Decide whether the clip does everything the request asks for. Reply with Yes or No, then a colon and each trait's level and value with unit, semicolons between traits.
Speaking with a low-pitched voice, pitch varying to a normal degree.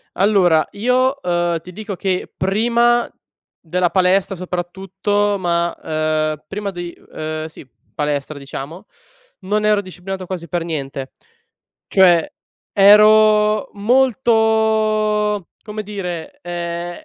No: high, 190 Hz; average, 3.7 semitones